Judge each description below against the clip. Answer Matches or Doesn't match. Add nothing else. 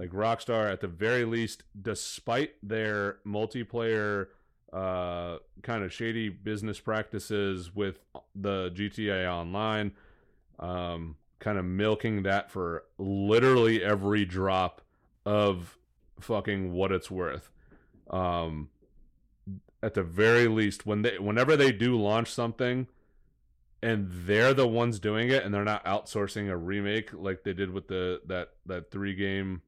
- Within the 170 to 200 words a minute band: Doesn't match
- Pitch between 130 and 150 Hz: Doesn't match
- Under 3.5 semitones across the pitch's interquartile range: Matches